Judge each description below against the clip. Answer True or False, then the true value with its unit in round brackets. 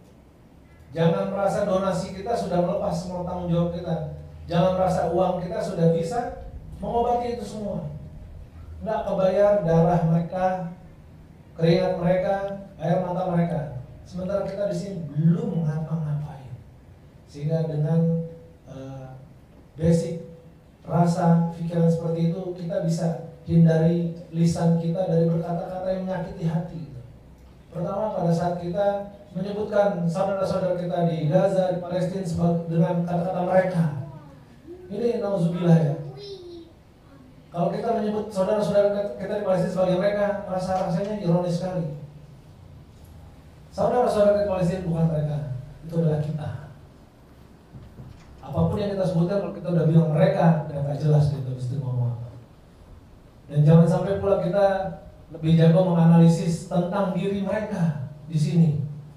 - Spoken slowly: False (120 wpm)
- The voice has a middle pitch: True (170 Hz)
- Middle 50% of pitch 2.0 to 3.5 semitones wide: True (3.1 semitones)